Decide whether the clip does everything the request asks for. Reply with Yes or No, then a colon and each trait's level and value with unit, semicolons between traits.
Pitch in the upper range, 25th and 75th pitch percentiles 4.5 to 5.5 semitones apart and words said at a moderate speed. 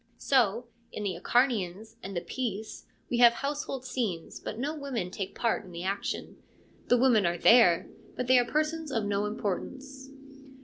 Yes: high, 235 Hz; average, 4.8 semitones; average, 170 wpm